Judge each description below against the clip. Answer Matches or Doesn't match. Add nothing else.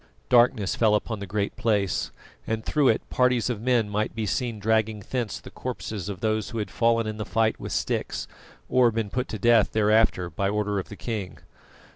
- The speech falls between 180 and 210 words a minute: Matches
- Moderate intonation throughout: Doesn't match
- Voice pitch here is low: Matches